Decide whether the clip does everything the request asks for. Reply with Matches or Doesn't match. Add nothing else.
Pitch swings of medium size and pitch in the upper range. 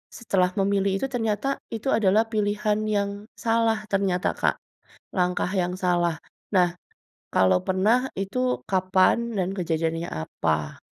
Matches